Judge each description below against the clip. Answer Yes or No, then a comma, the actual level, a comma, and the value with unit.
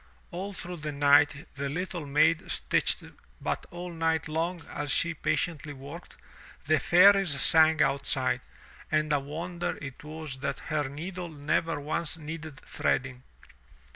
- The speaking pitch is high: No, medium, 155 Hz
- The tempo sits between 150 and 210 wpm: No, average, 140 wpm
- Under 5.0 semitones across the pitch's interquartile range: Yes, average, 2.8 semitones